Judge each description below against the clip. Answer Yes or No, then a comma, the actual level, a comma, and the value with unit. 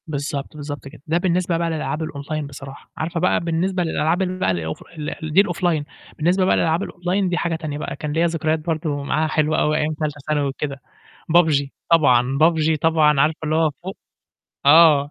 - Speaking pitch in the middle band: Yes, medium, 155 Hz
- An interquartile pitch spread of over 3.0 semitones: No, narrow, 2.5 semitones